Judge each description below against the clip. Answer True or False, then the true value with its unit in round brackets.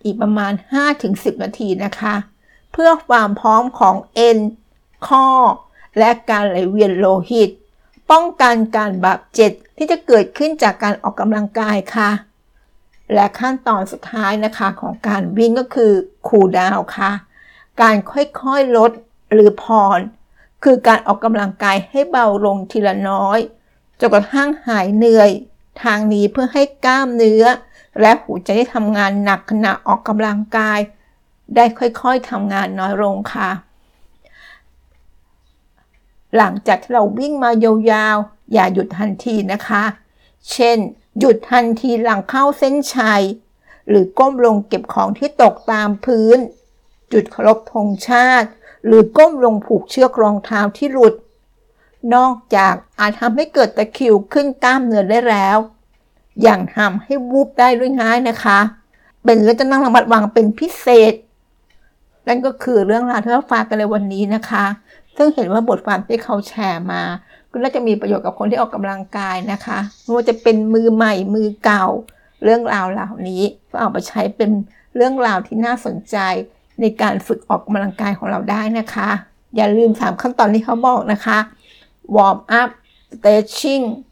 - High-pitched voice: True (220 Hz)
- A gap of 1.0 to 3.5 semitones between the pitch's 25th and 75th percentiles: True (2.8 semitones)